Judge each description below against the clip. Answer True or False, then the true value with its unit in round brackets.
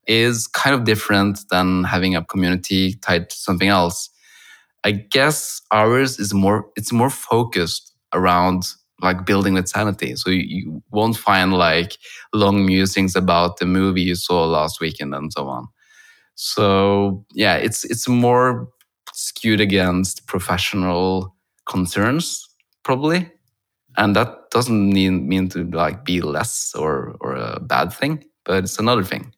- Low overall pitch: True (95 Hz)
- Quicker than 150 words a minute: False (145 wpm)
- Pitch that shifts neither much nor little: True (3.1 semitones)